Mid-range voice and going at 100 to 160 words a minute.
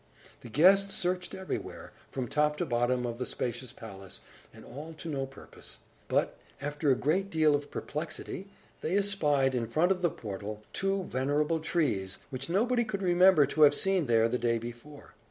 No: medium, 150 Hz; average, 175 wpm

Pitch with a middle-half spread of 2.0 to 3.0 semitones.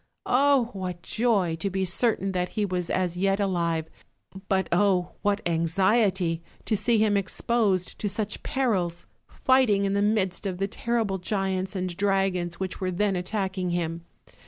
Yes: narrow, 2.6 semitones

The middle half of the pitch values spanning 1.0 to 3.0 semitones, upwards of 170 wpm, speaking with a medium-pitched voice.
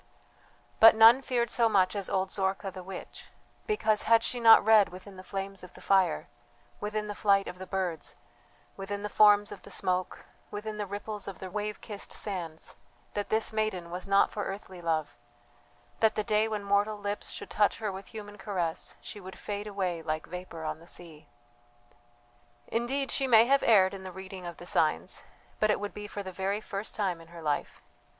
No: narrow, 2.4 semitones; average, 200 wpm; high, 200 Hz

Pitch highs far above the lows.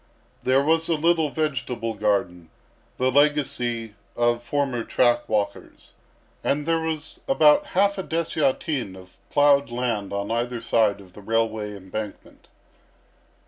Yes: wide, 5.7 semitones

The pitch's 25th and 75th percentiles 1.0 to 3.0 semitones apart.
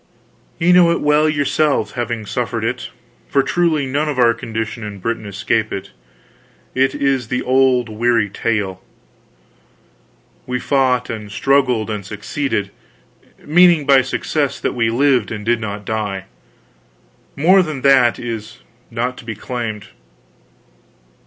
No: average, 4.1 semitones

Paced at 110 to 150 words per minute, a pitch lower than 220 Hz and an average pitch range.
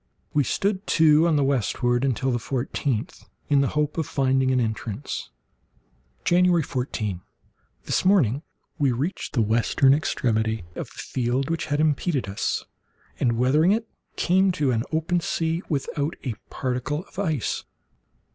Yes: average, 140 wpm; medium, 140 Hz; average, 4.7 semitones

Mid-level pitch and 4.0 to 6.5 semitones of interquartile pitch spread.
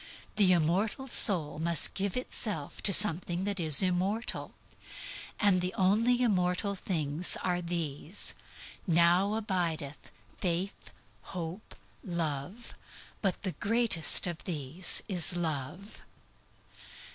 No: medium, 180 Hz; average, 3.4 semitones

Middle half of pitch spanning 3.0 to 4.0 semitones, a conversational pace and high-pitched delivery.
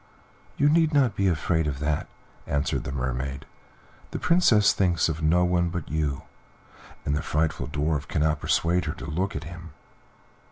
No: average, 3.5 semitones; average, 165 wpm; very low, 80 Hz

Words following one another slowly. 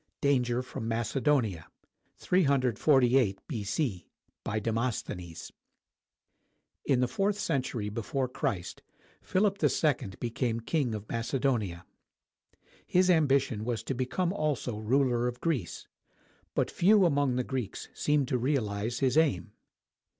Yes: slow, 115 wpm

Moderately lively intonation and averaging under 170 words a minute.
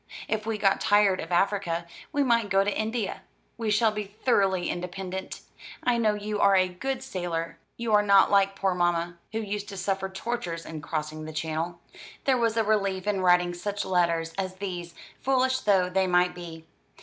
No: average, 3.2 semitones; average, 185 wpm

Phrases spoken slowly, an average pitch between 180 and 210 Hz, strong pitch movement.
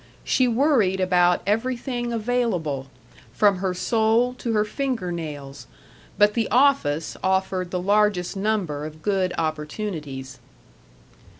Yes: slow, 115 wpm; high, 190 Hz; wide, 5.8 semitones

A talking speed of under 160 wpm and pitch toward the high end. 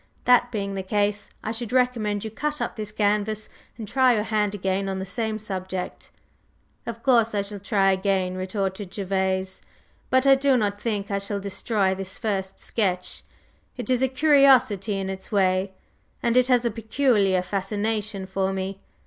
No: average, 175 wpm; high, 205 Hz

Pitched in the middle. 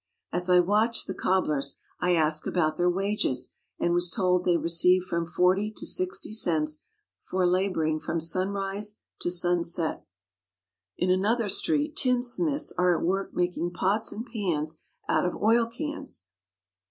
Yes: medium, 180 Hz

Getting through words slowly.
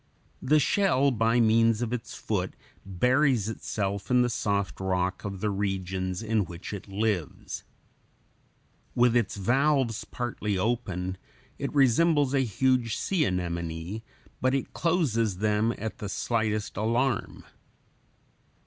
Yes: slow, 125 wpm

